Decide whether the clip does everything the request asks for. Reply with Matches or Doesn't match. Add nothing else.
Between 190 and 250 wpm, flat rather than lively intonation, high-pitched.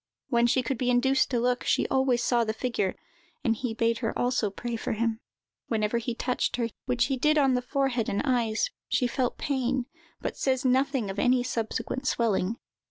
Matches